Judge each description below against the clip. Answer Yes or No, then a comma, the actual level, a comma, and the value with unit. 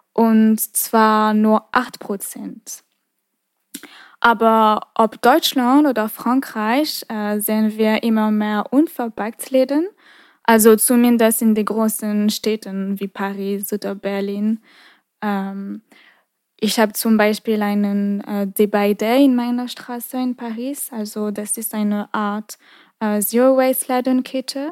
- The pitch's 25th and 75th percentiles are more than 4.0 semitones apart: No, average, 2.8 semitones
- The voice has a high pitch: Yes, high, 220 Hz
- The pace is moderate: No, slow, 115 wpm